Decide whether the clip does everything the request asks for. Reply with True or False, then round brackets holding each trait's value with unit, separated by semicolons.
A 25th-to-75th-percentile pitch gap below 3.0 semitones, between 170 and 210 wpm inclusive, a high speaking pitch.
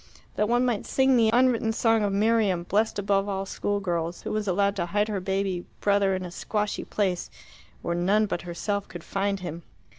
True (2.5 semitones; 200 wpm; 200 Hz)